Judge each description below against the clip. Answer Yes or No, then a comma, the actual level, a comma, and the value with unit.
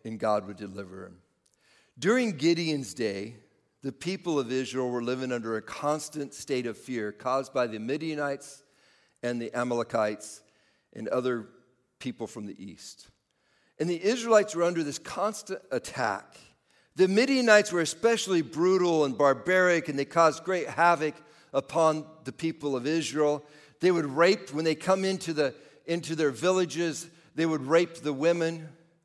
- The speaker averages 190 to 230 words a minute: No, average, 155 wpm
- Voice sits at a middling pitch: Yes, medium, 150 Hz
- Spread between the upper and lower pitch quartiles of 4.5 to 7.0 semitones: Yes, average, 5.0 semitones